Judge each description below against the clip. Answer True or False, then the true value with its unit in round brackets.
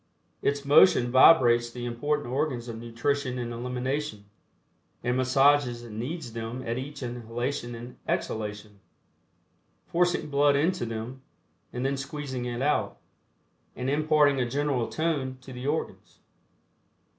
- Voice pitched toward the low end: True (130 Hz)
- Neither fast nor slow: False (130 wpm)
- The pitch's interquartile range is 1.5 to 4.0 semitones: True (3.2 semitones)